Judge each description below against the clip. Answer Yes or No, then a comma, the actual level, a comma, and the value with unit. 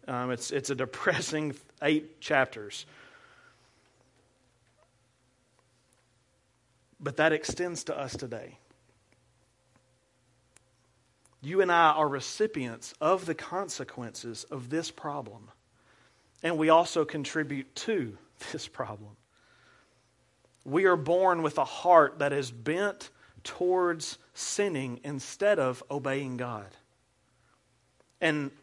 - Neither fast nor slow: No, slow, 100 wpm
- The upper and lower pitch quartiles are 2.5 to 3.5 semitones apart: No, average, 4.1 semitones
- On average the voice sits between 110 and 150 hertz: Yes, low, 135 Hz